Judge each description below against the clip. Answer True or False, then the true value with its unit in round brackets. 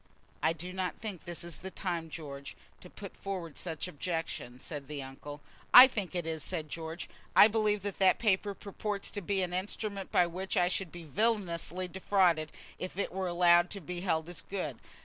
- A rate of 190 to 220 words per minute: True (195 wpm)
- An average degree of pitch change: True (3.1 semitones)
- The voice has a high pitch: False (180 Hz)